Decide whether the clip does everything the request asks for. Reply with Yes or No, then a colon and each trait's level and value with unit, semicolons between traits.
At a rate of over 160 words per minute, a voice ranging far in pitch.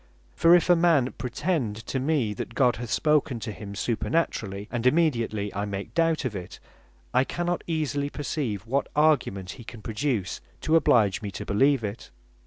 Yes: average, 180 wpm; wide, 6.5 semitones